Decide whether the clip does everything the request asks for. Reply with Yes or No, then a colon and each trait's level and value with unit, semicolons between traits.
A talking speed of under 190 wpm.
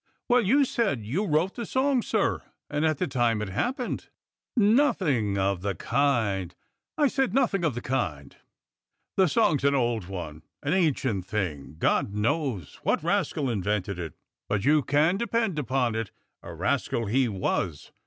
Yes: average, 165 wpm